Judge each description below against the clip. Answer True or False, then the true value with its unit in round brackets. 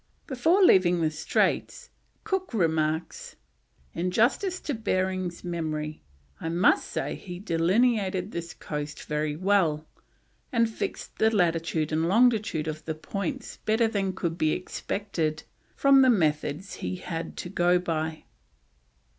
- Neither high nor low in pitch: True (180 Hz)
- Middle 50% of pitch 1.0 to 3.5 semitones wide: False (5.3 semitones)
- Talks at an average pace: False (130 wpm)